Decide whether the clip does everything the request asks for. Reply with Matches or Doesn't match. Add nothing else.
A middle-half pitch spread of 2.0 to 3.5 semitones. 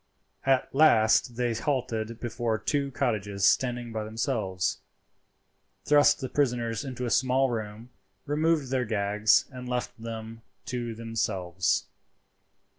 Matches